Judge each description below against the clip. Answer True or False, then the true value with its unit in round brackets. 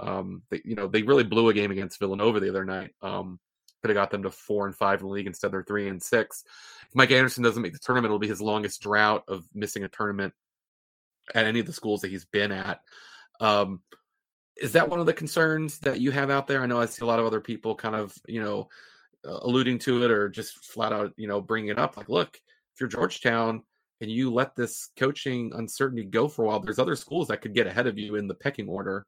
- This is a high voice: False (110 Hz)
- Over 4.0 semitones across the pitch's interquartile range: False (3.5 semitones)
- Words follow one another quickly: True (255 wpm)